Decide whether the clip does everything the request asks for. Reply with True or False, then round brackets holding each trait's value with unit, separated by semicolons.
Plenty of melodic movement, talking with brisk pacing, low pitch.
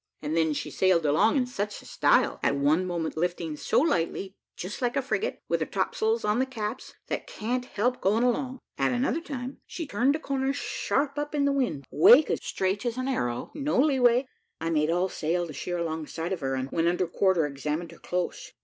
False (8.1 semitones; 215 wpm; 205 Hz)